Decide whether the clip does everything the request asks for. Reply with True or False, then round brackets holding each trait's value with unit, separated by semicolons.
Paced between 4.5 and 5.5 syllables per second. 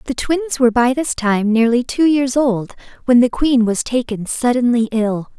True (4.6 syllables/s)